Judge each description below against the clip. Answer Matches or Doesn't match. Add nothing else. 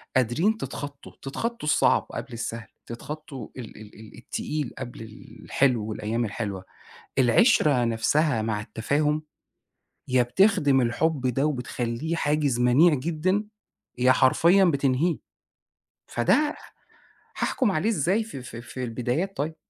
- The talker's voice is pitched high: Doesn't match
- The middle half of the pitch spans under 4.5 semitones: Doesn't match